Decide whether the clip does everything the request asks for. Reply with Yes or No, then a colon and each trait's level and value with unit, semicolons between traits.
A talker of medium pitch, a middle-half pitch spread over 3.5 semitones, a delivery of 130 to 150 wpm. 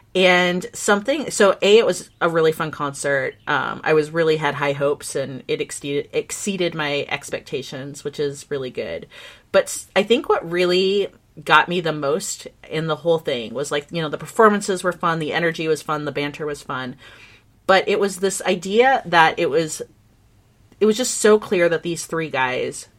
No: medium, 160 Hz; average, 4.9 semitones; average, 190 wpm